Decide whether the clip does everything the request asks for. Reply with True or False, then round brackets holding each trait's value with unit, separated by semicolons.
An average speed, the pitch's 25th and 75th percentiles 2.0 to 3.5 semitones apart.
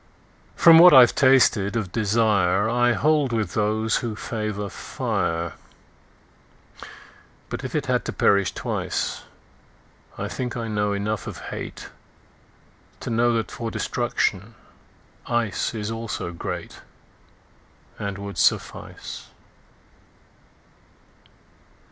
False (90 wpm; 2.7 semitones)